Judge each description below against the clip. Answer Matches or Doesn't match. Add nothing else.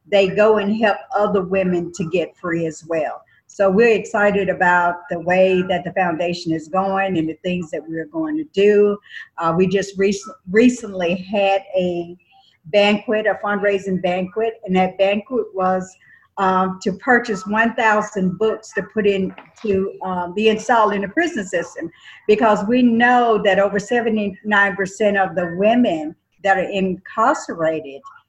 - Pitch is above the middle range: Matches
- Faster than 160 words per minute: Doesn't match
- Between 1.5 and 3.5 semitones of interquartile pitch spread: Matches